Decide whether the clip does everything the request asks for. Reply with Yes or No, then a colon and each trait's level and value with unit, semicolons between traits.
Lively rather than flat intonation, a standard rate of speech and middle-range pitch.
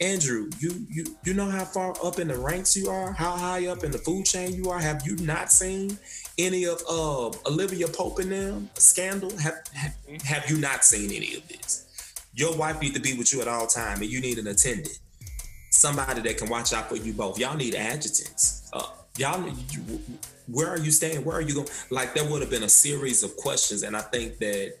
No: wide, 5.7 semitones; fast, 225 wpm; medium, 160 Hz